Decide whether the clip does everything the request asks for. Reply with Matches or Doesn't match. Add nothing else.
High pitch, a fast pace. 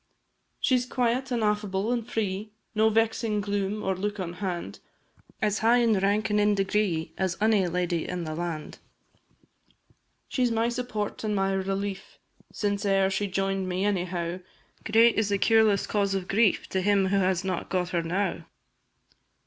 Doesn't match